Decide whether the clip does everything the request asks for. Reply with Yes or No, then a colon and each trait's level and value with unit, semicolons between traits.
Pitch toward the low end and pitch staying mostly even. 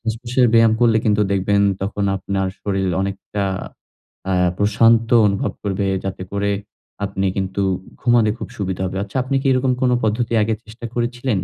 No: low, 105 Hz; average, 3.1 semitones